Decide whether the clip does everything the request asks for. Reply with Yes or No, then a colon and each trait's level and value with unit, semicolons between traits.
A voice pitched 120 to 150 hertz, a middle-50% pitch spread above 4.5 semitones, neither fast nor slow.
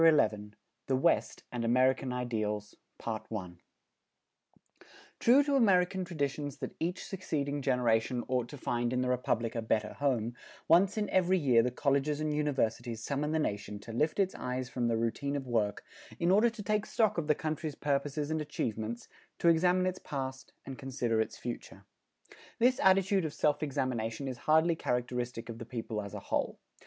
Yes: low, 135 Hz; average, 5.2 semitones; average, 170 wpm